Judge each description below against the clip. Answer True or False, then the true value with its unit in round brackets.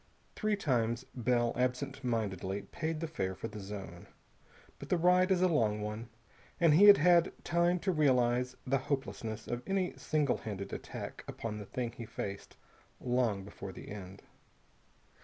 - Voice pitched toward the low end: True (125 Hz)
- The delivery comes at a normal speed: True (160 wpm)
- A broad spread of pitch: True (7.4 semitones)